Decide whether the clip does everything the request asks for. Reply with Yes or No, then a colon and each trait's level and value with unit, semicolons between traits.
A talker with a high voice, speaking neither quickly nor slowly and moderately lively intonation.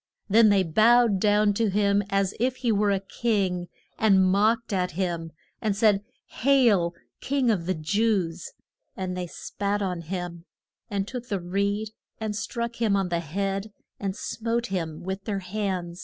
Yes: high, 200 Hz; average, 165 wpm; average, 3.0 semitones